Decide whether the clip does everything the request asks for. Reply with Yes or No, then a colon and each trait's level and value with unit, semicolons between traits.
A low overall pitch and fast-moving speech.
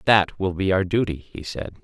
Yes: very low, 95 Hz; fast, 230 wpm